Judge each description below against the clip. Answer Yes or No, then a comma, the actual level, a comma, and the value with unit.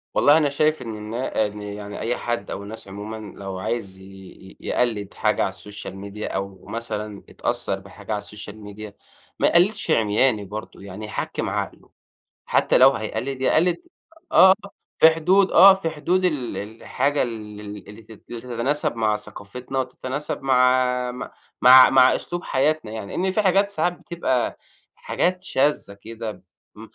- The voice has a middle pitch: No, low, 115 Hz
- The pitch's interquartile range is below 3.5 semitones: No, wide, 5.5 semitones